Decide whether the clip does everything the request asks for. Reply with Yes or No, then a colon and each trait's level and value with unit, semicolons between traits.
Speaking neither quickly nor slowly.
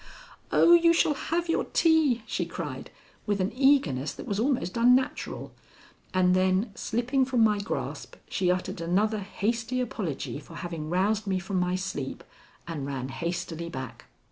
Yes: average, 155 wpm